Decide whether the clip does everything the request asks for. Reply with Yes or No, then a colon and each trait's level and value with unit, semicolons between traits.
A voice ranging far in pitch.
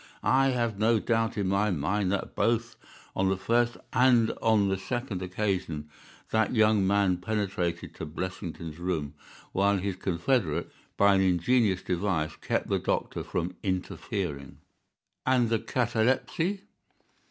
No: average, 4.0 semitones